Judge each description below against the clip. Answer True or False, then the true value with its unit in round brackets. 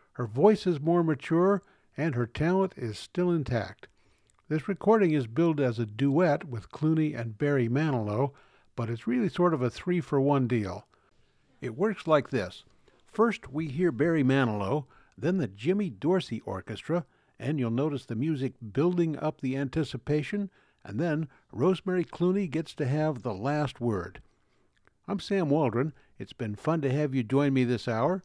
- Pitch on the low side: False (150 Hz)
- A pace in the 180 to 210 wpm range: False (165 wpm)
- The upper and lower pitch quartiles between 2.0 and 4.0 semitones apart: False (5.6 semitones)